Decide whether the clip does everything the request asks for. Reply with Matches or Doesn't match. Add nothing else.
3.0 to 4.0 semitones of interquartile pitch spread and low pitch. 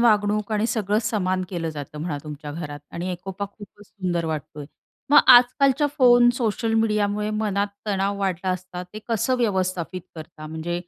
Doesn't match